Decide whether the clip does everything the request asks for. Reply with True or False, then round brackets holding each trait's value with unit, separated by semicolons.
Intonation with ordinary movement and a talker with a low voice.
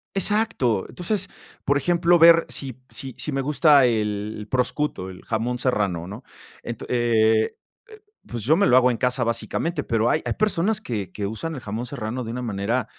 False (5.8 semitones; 125 Hz)